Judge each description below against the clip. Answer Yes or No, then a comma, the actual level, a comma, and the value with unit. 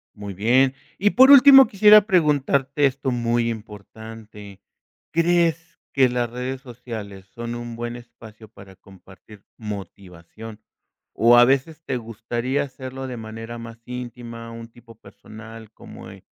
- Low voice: Yes, low, 120 Hz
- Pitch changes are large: No, average, 3.2 semitones